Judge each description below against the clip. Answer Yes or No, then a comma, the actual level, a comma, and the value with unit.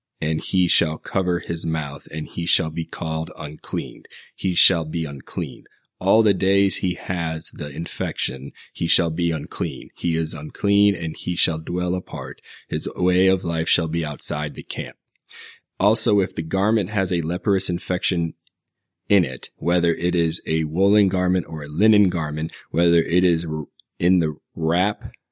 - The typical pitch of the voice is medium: No, very low, 85 Hz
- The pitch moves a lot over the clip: No, narrow, 2.5 semitones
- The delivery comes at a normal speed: Yes, average, 165 wpm